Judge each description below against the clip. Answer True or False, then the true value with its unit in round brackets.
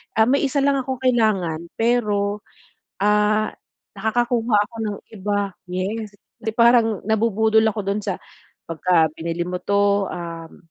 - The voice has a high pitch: True (210 Hz)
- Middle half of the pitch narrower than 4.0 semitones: True (2.7 semitones)